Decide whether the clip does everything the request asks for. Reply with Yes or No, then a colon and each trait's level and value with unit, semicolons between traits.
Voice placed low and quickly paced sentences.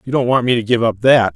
Yes: low, 120 Hz; fast, 355 wpm